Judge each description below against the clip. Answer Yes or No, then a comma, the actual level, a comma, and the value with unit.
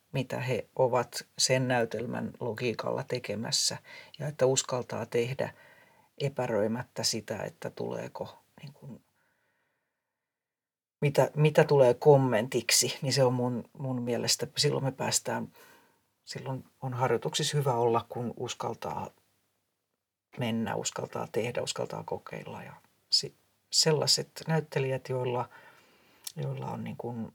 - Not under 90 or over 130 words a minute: Yes, average, 110 wpm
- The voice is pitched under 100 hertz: No, low, 130 Hz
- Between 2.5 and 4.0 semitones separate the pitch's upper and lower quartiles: Yes, average, 3.2 semitones